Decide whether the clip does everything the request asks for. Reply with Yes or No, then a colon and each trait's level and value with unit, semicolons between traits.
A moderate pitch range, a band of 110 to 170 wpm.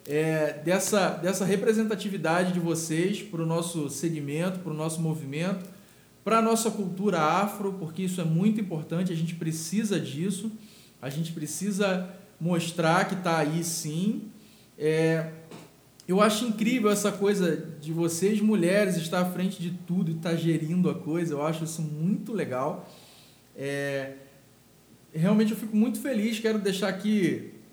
Yes: average, 4.0 semitones; average, 150 wpm